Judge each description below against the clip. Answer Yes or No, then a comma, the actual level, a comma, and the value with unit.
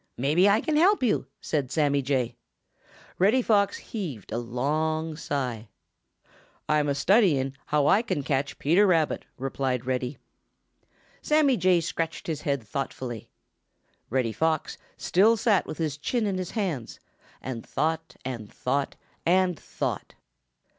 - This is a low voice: No, medium, 150 Hz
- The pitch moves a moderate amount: No, wide, 6.0 semitones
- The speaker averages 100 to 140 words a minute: Yes, slow, 135 wpm